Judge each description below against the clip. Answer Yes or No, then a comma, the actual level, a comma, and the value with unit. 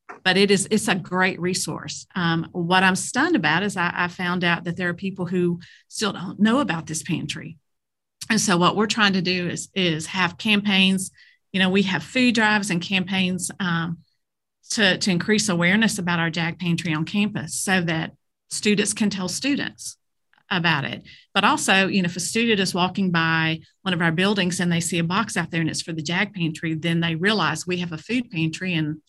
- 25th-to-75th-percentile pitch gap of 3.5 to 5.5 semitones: No, average, 3.0 semitones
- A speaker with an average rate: No, fast, 210 wpm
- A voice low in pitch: No, medium, 180 Hz